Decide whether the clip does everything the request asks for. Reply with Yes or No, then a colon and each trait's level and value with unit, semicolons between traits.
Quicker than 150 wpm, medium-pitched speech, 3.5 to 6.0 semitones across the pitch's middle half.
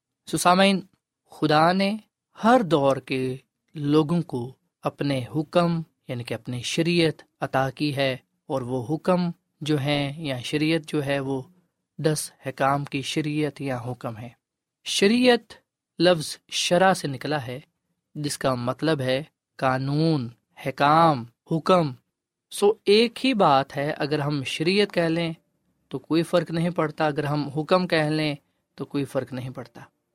No: average, 145 wpm; medium, 150 Hz; average, 3.8 semitones